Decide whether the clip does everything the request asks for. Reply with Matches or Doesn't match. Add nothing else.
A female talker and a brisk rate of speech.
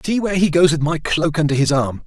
Doesn't match